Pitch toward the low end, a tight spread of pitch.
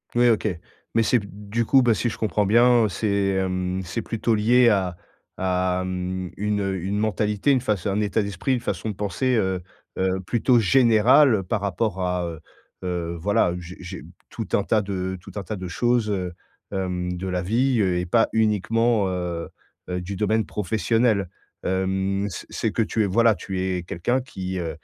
No: low, 100 Hz; average, 3.4 semitones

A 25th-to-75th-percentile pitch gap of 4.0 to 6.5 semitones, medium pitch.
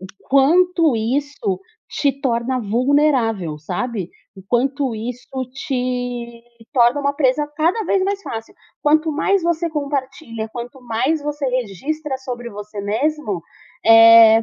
No: average, 4.5 semitones; very high, 255 Hz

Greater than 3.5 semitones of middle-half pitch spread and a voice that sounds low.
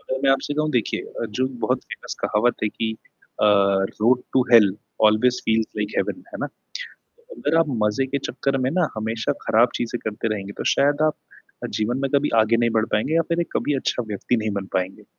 Yes: average, 4.4 semitones; low, 120 Hz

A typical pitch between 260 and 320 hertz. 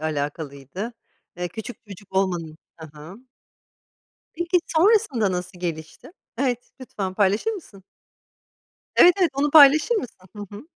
No: high, 200 Hz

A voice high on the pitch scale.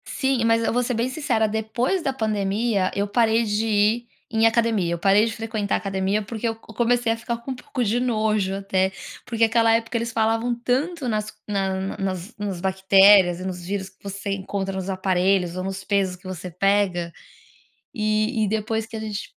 Yes: high, 215 Hz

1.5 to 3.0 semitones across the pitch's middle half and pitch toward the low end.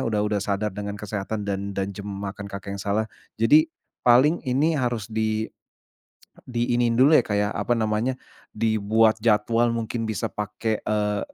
Yes: narrow, 2.4 semitones; low, 110 Hz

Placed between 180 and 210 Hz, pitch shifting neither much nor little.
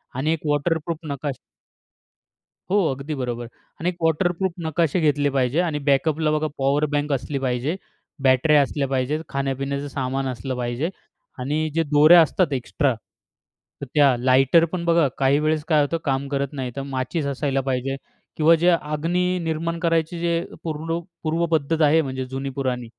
No: medium, 145 Hz; average, 3.2 semitones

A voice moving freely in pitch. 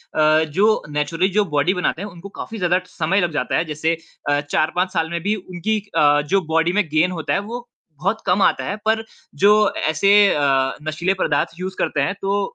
No: average, 4.2 semitones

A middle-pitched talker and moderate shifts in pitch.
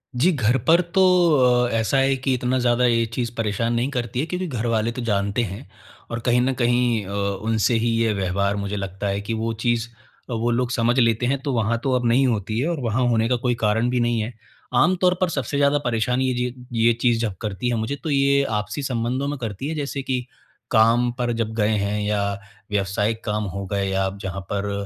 No: low, 115 Hz; average, 3.0 semitones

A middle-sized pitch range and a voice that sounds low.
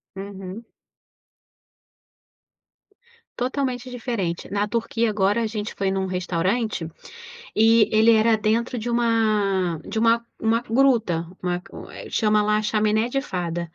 No: average, 3.2 semitones; high, 215 Hz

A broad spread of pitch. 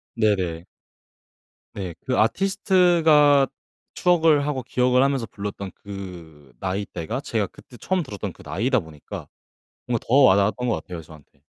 Yes: wide, 6.9 semitones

